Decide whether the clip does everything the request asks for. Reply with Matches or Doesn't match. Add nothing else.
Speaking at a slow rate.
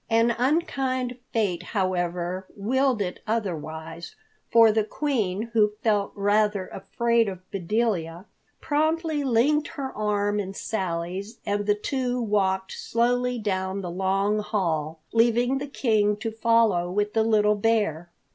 Matches